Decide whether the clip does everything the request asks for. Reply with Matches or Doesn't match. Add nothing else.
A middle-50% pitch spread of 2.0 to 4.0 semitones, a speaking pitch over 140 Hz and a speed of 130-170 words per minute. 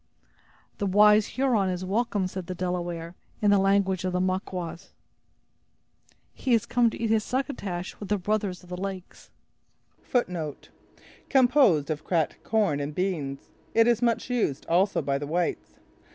Matches